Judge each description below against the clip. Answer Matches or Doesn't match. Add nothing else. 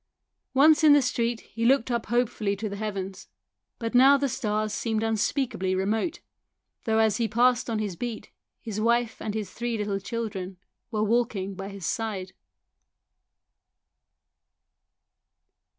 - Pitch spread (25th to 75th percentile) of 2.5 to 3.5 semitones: Matches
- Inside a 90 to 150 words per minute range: Matches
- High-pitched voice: Matches